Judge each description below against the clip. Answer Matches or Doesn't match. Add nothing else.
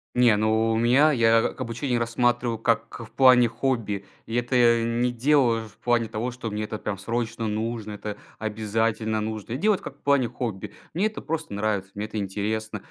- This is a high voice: Doesn't match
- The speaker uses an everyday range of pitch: Doesn't match